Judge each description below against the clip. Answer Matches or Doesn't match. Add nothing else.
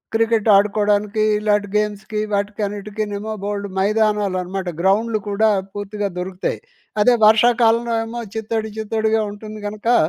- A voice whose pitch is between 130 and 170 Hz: Doesn't match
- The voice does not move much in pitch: Matches